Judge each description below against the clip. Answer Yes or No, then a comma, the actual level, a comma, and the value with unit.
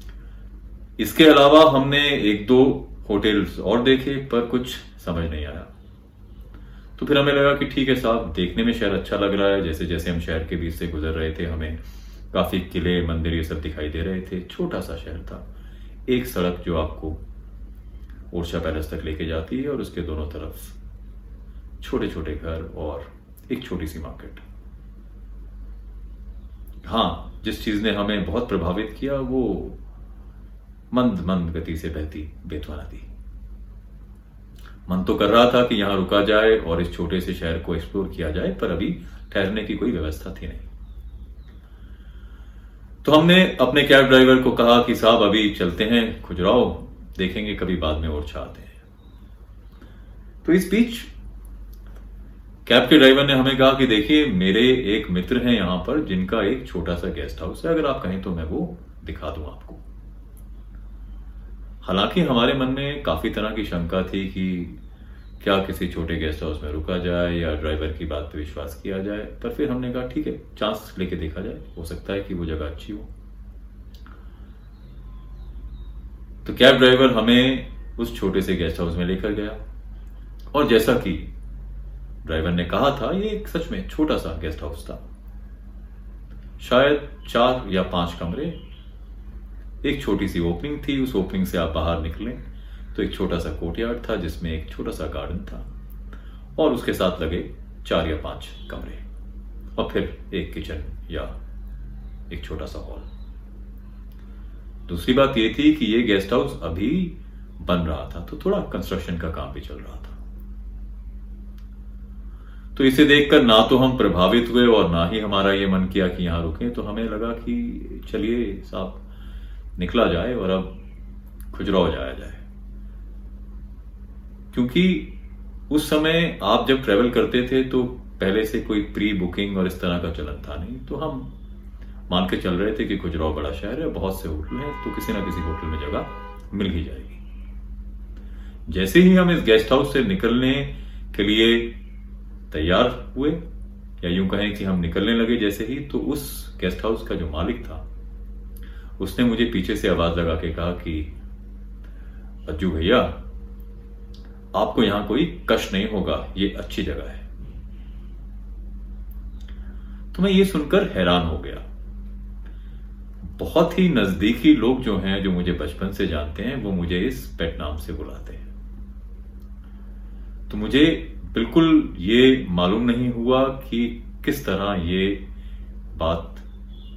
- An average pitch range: No, wide, 7.9 semitones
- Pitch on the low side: Yes, very low, 90 Hz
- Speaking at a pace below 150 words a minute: No, average, 160 wpm